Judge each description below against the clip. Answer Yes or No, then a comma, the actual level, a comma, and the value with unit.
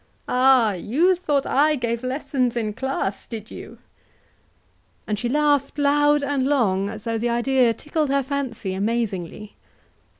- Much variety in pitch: No, average, 4.2 semitones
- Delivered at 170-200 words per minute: No, average, 140 wpm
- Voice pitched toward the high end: Yes, very high, 255 Hz